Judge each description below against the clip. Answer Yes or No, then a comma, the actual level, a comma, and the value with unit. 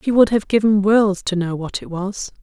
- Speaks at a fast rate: Yes, fast, 250 wpm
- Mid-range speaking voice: No, high, 200 Hz